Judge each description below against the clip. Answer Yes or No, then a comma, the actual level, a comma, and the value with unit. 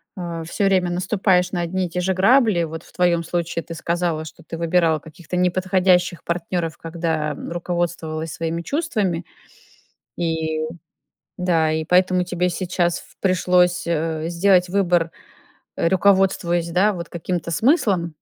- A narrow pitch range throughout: Yes, narrow, 1.7 semitones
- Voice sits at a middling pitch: Yes, medium, 175 Hz